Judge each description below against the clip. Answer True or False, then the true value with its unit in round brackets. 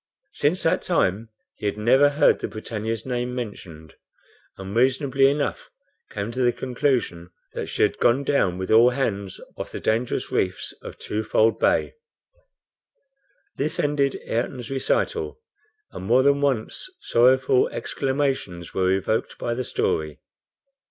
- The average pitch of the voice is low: True (120 Hz)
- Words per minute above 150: False (140 wpm)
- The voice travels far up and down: False (4.4 semitones)